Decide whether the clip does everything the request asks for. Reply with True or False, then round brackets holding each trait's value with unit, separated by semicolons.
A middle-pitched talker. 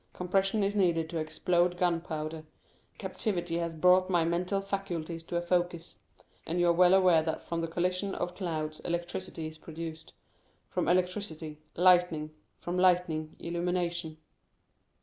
True (175 Hz)